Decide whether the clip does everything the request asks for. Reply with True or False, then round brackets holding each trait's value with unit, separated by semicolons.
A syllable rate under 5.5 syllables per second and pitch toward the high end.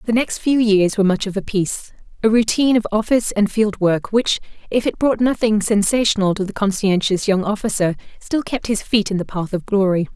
False (5.6 syllables/s; 210 Hz)